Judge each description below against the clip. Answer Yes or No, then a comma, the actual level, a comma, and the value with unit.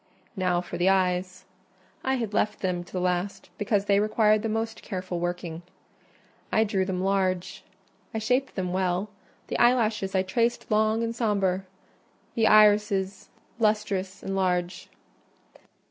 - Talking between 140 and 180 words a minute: Yes, average, 145 wpm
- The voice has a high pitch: Yes, high, 195 Hz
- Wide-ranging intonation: No, average, 2.7 semitones